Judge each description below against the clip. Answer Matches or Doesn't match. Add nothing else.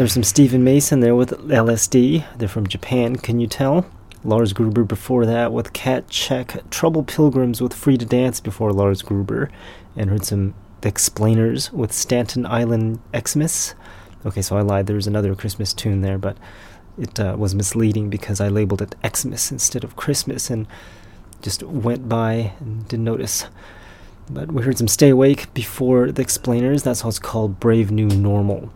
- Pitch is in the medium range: Doesn't match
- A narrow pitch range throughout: Doesn't match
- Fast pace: Doesn't match